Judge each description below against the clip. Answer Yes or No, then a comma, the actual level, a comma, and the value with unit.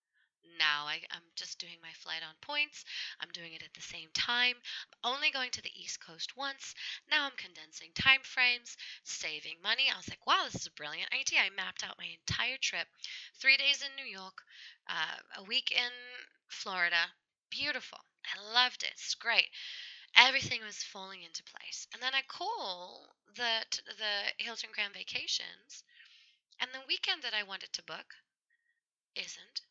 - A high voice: Yes, high, 245 Hz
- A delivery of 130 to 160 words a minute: No, average, 170 wpm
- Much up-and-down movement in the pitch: Yes, wide, 6.1 semitones